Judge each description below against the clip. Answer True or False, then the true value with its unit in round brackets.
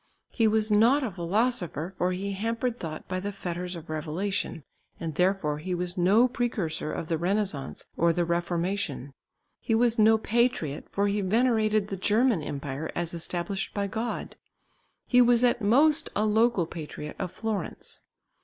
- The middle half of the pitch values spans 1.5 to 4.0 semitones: False (4.7 semitones)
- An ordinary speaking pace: True (160 wpm)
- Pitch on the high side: True (195 Hz)